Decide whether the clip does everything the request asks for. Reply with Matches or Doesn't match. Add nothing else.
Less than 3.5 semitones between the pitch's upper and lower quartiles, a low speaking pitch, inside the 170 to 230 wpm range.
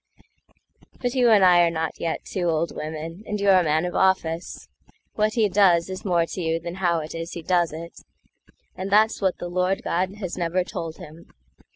Doesn't match